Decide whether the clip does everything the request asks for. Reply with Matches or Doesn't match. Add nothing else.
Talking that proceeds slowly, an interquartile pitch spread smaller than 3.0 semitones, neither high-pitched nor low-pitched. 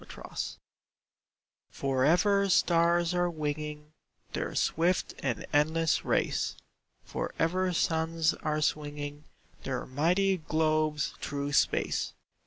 Matches